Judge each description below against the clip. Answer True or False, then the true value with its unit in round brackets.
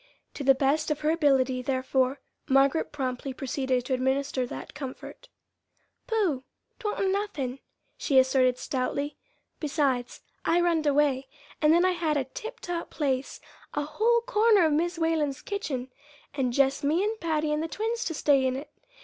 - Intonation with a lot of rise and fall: False (4.1 semitones)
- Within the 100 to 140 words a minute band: False (160 wpm)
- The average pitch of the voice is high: True (290 Hz)